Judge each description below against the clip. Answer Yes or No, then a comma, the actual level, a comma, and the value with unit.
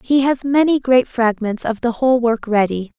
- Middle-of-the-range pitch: No, high, 240 Hz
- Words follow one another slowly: No, average, 200 wpm